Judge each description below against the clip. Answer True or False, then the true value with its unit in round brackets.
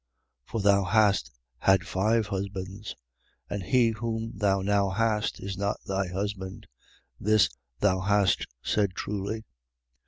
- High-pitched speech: False (100 Hz)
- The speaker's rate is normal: False (130 wpm)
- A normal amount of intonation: False (1.9 semitones)